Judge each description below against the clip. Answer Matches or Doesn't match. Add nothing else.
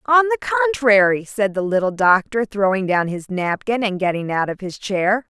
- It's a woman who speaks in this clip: Matches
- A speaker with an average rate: Matches